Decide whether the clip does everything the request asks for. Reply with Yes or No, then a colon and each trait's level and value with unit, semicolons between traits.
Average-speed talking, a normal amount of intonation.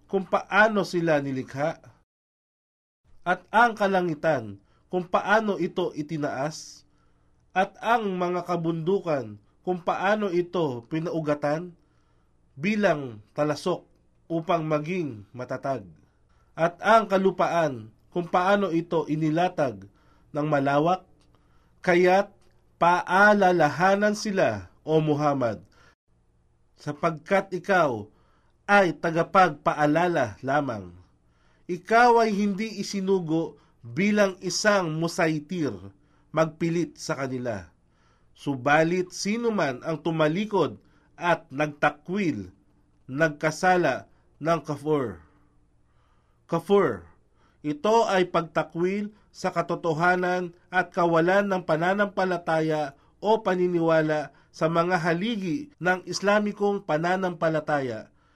No: slow, 85 wpm; average, 4.1 semitones